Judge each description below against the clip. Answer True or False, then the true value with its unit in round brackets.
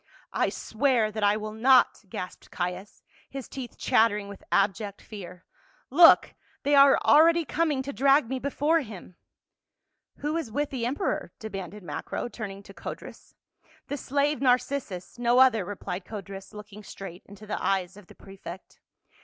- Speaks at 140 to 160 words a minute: False (170 wpm)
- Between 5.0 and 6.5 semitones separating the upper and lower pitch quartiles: True (5.6 semitones)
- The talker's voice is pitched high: True (220 Hz)